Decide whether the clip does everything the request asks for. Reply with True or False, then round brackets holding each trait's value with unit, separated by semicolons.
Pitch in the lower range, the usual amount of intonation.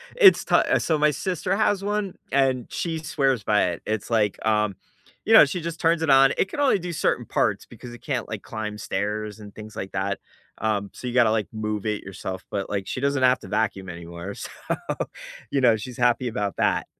False (115 Hz; 6.0 semitones)